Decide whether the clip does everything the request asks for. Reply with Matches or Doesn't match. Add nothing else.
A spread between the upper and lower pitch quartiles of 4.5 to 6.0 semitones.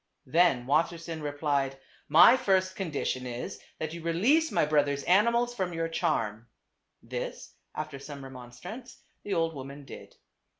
Matches